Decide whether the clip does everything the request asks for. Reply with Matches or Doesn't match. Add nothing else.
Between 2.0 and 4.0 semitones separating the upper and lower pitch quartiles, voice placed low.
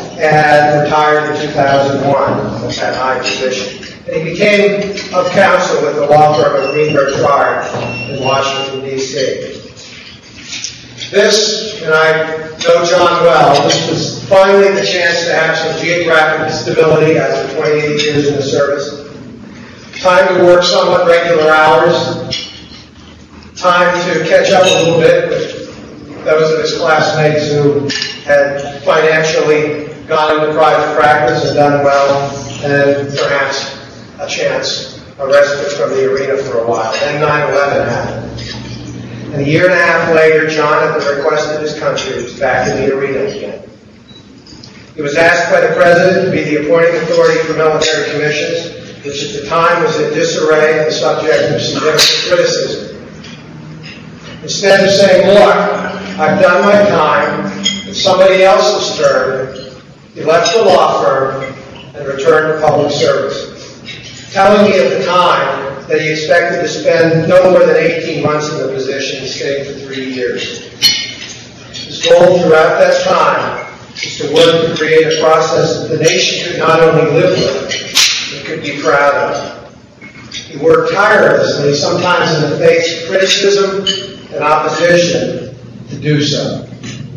Doesn't match